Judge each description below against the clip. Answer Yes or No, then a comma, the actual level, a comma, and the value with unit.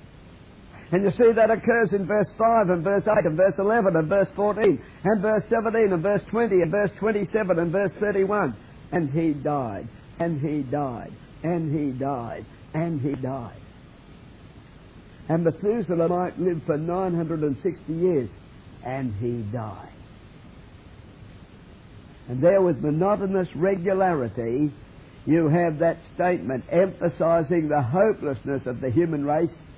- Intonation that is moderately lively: No, wide, 6.0 semitones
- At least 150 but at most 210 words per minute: No, slow, 135 wpm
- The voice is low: No, medium, 165 Hz